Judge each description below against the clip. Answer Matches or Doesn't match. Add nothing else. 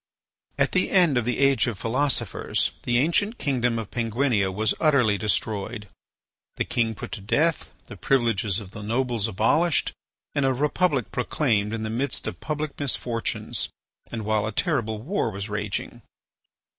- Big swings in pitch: Doesn't match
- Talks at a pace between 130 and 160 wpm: Matches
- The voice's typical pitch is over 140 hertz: Doesn't match